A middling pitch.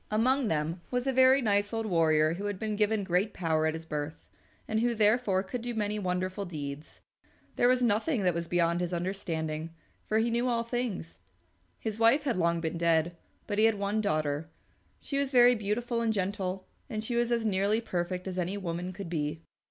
No: high, 200 Hz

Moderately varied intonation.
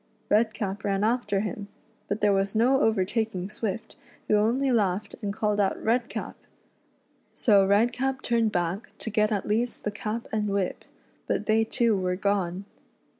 No: narrow, 2.2 semitones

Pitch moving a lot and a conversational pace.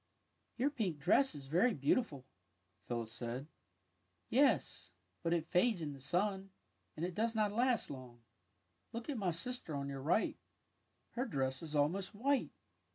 Yes: wide, 8.5 semitones; average, 170 wpm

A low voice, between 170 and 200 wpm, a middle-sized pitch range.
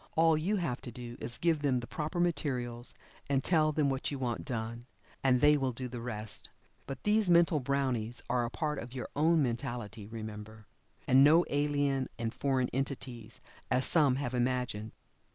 Yes: low, 130 Hz; average, 185 wpm; average, 3.7 semitones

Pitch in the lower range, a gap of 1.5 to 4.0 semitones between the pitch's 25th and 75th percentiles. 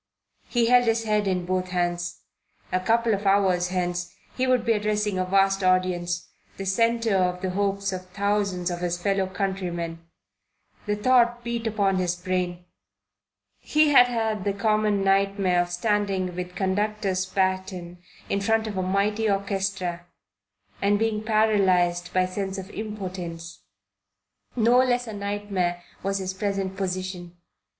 No: high, 195 Hz; narrow, 2.6 semitones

